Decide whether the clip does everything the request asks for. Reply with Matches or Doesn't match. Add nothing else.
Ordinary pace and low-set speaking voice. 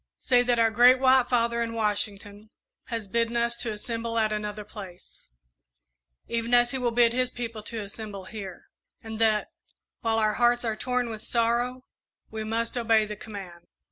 Doesn't match